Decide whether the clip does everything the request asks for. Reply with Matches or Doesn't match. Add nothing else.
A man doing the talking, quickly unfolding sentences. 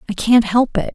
Doesn't match